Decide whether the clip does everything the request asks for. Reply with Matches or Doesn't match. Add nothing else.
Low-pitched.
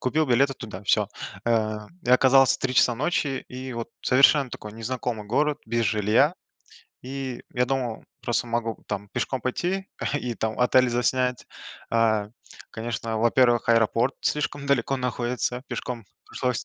Matches